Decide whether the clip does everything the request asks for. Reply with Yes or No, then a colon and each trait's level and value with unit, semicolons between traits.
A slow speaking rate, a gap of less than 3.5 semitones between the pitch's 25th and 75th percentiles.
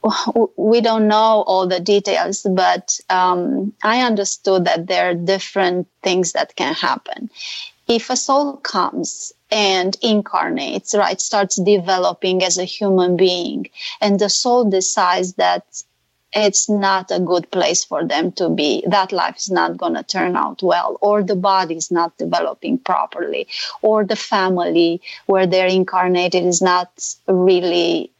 No: average, 150 wpm; average, 2.8 semitones